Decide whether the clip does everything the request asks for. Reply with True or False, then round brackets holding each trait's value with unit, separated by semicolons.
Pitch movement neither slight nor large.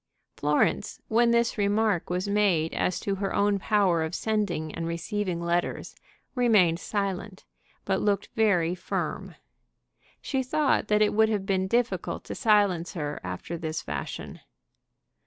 True (3.8 semitones)